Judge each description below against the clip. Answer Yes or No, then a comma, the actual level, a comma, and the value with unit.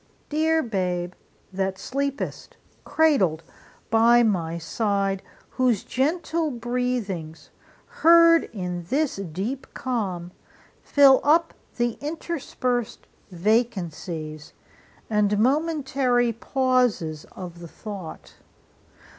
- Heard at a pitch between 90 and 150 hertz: No, high, 230 Hz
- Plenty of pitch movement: Yes, wide, 6.8 semitones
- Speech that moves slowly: Yes, slow, 85 wpm